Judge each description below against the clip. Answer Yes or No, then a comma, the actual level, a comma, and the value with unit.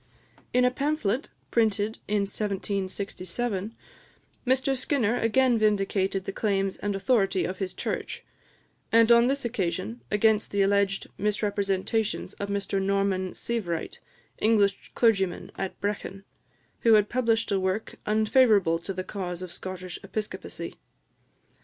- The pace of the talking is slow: Yes, slow, 125 wpm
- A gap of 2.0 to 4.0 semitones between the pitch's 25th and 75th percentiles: Yes, average, 2.7 semitones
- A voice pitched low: No, high, 200 Hz